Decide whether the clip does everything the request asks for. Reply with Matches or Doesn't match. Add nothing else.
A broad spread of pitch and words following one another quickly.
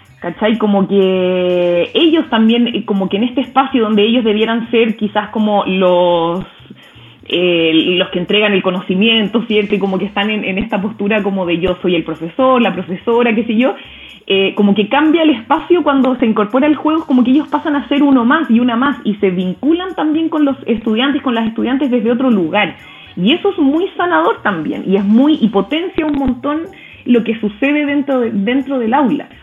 Matches